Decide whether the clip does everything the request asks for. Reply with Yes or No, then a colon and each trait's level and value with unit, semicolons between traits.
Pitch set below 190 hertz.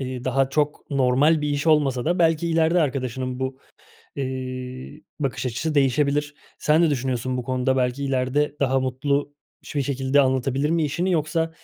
Yes: low, 135 Hz